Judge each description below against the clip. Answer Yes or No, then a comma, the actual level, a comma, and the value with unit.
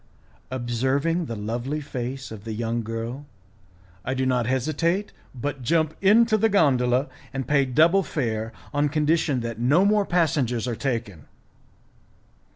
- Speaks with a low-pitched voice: Yes, low, 130 Hz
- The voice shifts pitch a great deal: No, average, 4.9 semitones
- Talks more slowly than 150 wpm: Yes, average, 140 wpm